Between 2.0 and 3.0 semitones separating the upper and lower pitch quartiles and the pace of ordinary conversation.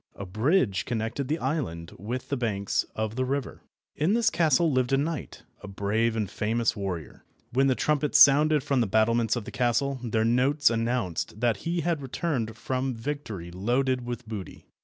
No: average, 4.2 semitones; average, 180 wpm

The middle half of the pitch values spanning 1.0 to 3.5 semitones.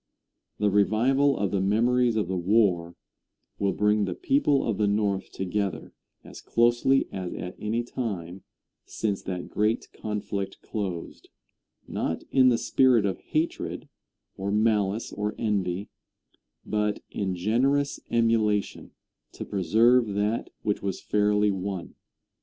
Yes: average, 3.0 semitones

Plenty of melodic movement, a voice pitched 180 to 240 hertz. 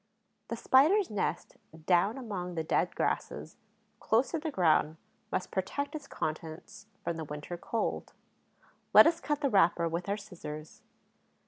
Yes: wide, 8.2 semitones; high, 190 Hz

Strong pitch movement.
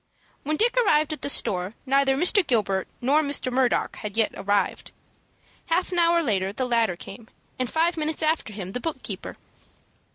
Yes: wide, 6.8 semitones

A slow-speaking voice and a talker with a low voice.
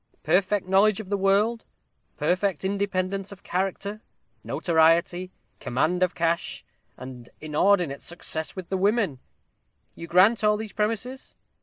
No: slow, 125 wpm; high, 190 Hz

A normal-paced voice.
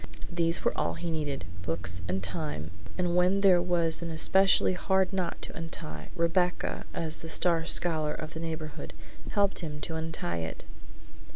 Yes: average, 165 wpm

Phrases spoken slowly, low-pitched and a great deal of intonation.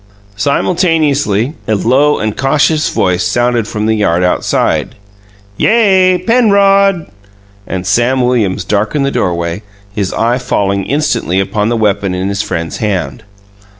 Yes: slow, 130 wpm; low, 115 Hz; wide, 7.2 semitones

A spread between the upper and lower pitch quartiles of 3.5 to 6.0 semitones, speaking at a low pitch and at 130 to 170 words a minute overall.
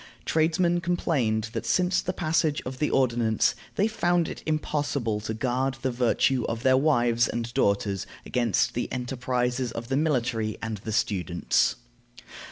Yes: average, 5.0 semitones; low, 125 Hz; average, 150 wpm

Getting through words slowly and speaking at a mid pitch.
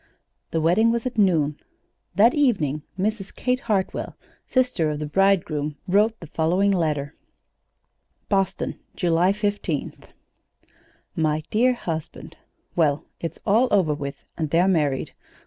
Yes: slow, 125 wpm; medium, 180 Hz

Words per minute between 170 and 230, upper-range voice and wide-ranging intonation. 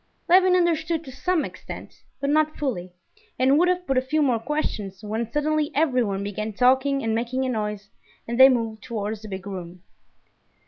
Yes: average, 180 wpm; very high, 255 Hz; wide, 6.0 semitones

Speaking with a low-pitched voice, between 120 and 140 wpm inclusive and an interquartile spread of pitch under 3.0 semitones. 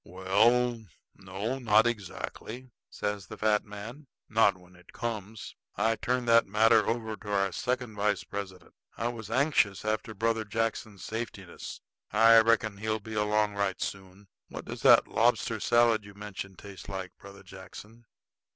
No: low, 105 Hz; average, 150 wpm; narrow, 2.4 semitones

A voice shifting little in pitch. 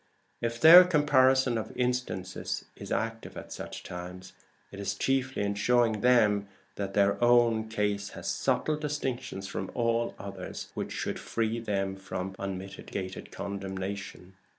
No: average, 3.9 semitones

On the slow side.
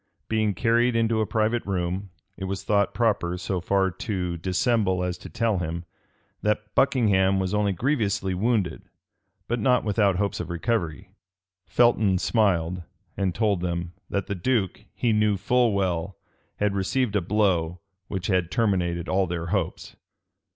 No: average, 150 wpm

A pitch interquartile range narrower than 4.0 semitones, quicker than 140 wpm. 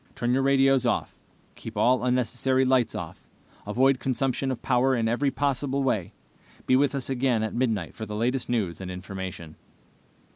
Yes: average, 3.2 semitones; average, 170 wpm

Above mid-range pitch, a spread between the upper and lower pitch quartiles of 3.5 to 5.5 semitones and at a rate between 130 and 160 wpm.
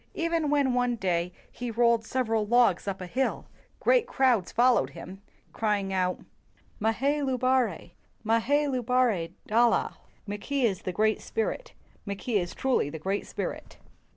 Yes: high, 230 Hz; average, 4.6 semitones; slow, 135 wpm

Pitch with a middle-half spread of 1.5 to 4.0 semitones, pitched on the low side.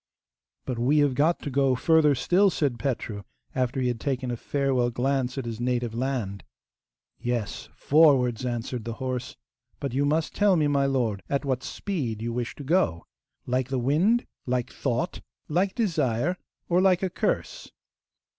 Yes: average, 3.6 semitones; low, 130 Hz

